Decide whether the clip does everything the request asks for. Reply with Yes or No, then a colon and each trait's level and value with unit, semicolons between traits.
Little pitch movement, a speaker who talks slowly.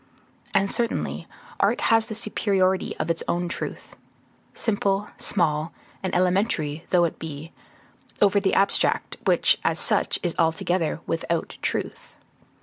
No: average, 3.3 semitones; slow, 130 wpm